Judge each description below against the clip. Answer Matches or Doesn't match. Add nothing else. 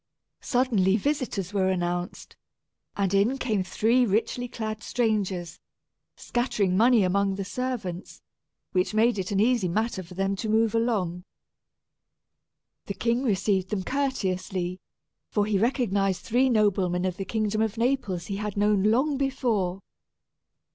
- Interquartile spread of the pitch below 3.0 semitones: Doesn't match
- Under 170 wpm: Matches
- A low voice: Doesn't match